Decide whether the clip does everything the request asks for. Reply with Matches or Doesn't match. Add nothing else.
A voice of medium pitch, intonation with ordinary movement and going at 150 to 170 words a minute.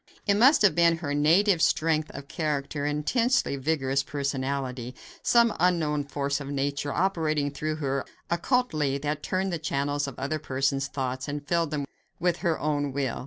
Matches